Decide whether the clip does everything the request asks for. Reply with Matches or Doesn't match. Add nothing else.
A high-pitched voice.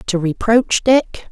Matches